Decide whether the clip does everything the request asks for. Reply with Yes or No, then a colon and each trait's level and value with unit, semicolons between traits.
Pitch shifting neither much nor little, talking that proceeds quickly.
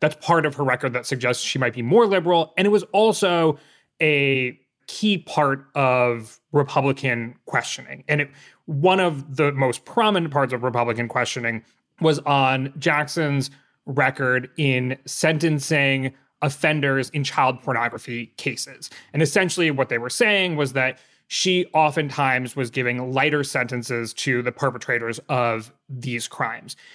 No: average, 3.6 semitones; average, 145 wpm